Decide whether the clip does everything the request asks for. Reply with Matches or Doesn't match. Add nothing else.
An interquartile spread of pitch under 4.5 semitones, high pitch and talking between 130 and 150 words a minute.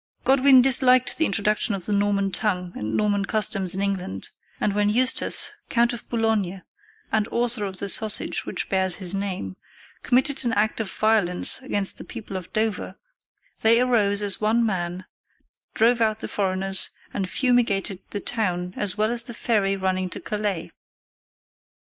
Doesn't match